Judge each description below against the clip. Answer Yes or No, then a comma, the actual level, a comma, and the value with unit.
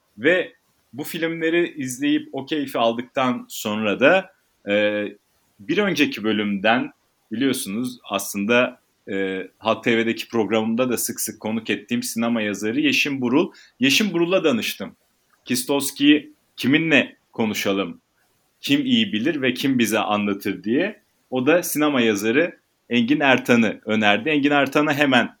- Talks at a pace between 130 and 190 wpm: No, average, 120 wpm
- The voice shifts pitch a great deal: Yes, wide, 5.8 semitones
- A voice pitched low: Yes, low, 130 Hz